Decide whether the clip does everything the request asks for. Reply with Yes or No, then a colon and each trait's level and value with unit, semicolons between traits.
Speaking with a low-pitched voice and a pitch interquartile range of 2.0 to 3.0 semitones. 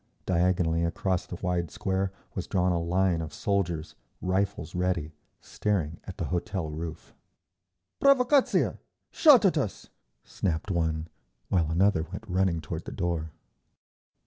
Yes: very low, 90 Hz; average, 2.7 semitones